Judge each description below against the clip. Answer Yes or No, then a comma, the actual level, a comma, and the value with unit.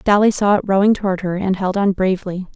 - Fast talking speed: Yes, fast, 235 wpm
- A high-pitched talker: Yes, high, 195 Hz